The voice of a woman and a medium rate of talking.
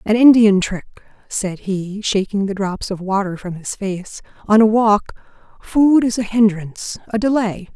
Yes: female; average, 170 wpm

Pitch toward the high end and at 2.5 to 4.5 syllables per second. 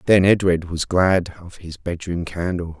No: very low, 90 Hz; 4.3 syllables/s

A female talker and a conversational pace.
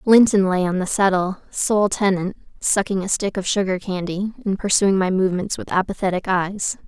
Yes: female; average, 175 wpm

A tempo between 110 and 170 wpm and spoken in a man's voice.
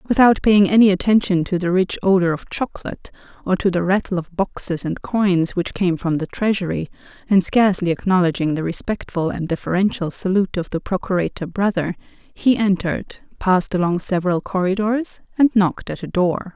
No: average, 165 wpm; female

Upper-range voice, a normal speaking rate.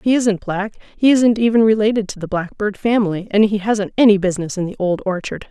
No: high, 205 Hz; fast, 220 wpm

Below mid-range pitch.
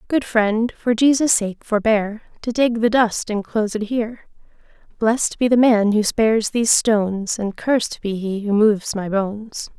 No: high, 220 Hz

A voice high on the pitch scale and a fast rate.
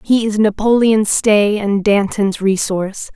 No: high, 205 Hz; slow, 135 wpm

